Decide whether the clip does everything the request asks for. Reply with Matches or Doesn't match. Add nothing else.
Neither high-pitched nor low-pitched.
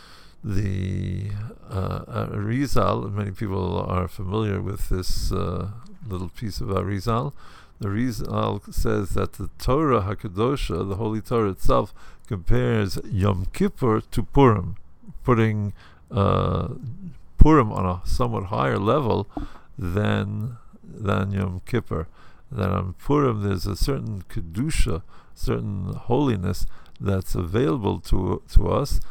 Doesn't match